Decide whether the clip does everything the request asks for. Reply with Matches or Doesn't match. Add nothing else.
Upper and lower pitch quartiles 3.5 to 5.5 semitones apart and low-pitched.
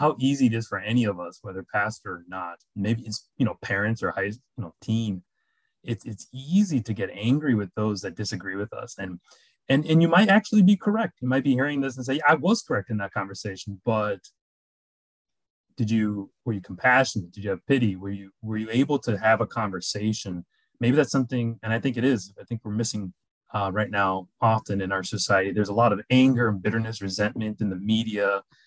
Matches